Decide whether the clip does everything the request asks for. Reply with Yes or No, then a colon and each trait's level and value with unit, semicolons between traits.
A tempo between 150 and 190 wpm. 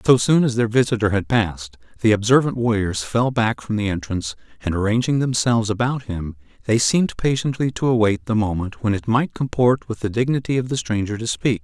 No: average, 200 wpm